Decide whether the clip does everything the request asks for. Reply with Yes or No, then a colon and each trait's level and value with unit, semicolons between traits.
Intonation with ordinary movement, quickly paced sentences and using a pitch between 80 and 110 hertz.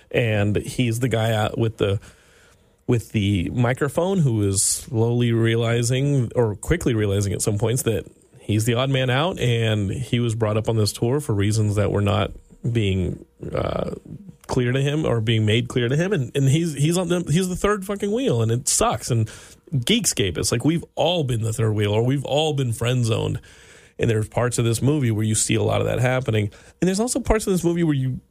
No: average, 4.7 semitones; fast, 220 wpm; low, 120 Hz